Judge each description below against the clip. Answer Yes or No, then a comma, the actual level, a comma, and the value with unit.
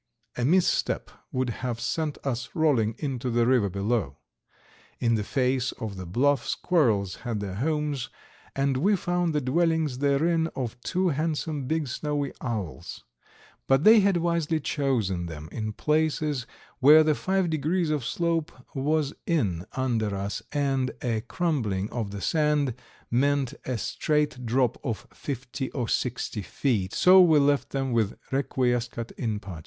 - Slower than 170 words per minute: Yes, average, 150 wpm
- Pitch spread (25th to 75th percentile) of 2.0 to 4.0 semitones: No, average, 4.9 semitones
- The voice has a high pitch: No, low, 135 Hz